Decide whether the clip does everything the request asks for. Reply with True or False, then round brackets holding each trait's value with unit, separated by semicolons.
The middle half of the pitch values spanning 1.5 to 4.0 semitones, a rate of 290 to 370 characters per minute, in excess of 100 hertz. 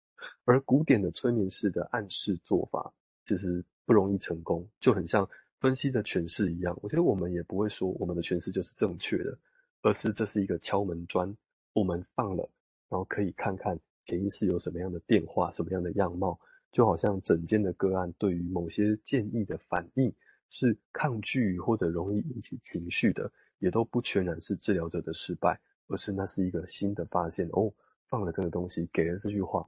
False (3.6 semitones; 300 characters per minute; 95 Hz)